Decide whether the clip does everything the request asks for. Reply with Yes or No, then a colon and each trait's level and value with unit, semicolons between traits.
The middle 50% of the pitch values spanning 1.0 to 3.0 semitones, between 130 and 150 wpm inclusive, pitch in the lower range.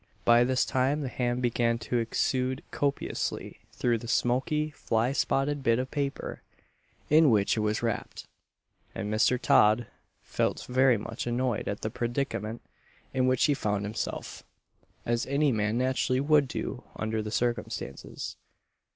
Yes: average, 2.7 semitones; average, 145 wpm; low, 120 Hz